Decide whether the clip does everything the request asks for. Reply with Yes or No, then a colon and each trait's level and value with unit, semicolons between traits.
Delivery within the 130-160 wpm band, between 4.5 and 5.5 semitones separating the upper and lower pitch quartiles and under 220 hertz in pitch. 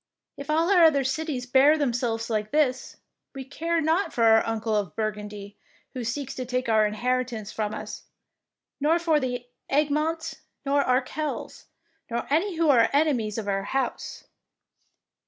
No: average, 155 wpm; average, 5.2 semitones; very high, 255 Hz